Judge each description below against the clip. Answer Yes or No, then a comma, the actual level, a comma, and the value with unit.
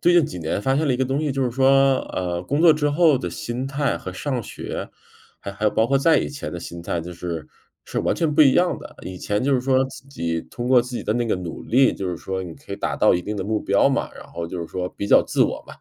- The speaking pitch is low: Yes, low, 125 Hz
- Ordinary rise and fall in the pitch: No, wide, 6.9 semitones